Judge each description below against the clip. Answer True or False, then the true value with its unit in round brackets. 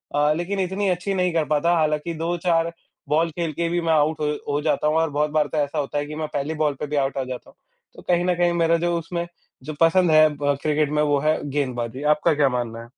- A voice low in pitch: False (155 Hz)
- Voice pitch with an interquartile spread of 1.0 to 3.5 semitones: True (2.5 semitones)